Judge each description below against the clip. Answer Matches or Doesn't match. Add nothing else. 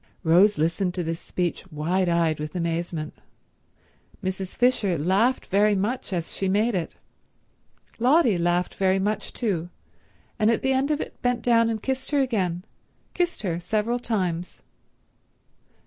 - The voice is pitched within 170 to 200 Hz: Matches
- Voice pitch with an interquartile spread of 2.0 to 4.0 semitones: Doesn't match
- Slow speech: Doesn't match